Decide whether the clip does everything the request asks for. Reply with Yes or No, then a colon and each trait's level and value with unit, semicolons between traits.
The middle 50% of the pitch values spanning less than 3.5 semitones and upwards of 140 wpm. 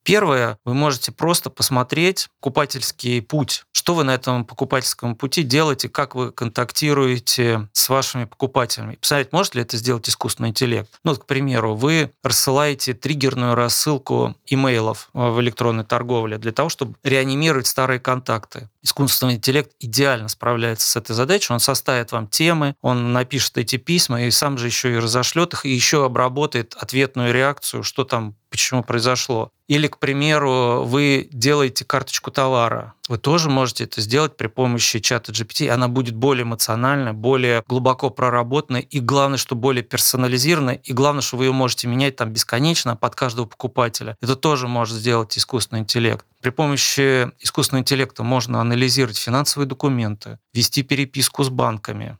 Yes: narrow, 2.6 semitones; average, 155 wpm